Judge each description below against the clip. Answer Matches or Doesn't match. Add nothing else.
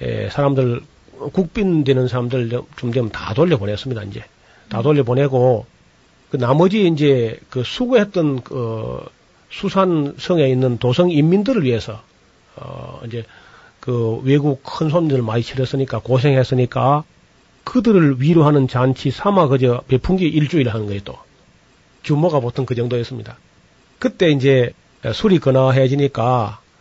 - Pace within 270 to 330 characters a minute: Matches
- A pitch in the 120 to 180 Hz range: Matches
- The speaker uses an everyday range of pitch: Matches